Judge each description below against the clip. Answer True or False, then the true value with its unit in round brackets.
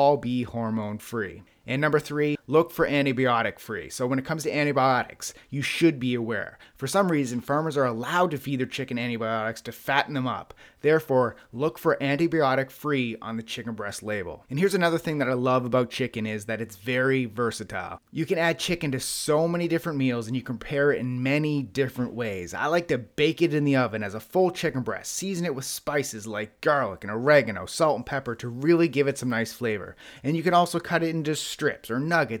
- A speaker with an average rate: False (220 wpm)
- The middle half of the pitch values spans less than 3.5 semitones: False (4.3 semitones)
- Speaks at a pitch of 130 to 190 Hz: True (135 Hz)